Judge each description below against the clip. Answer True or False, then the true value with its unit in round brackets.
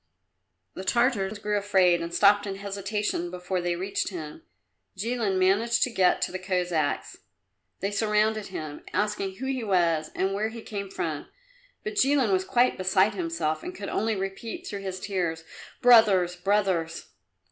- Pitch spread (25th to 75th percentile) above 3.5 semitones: False (2.9 semitones)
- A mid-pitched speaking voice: False (195 Hz)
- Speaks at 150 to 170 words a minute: True (160 wpm)